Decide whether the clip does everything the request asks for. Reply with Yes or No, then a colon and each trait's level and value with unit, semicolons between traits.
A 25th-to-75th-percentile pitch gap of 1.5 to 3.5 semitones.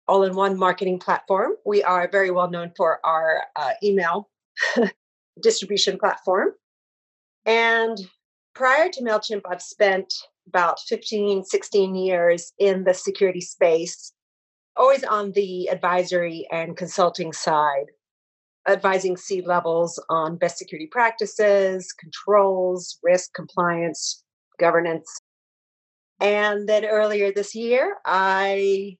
Yes: average, 2.9 semitones